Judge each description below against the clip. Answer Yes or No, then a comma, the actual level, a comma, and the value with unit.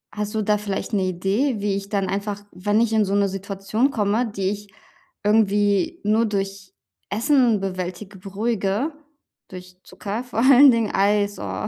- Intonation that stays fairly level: Yes, narrow, 2.1 semitones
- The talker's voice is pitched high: Yes, high, 205 Hz